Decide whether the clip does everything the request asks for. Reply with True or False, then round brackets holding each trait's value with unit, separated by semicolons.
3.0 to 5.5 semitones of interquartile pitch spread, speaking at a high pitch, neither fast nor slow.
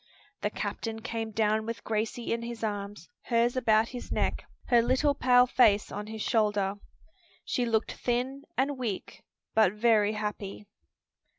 False (2.4 semitones; 225 Hz; 150 wpm)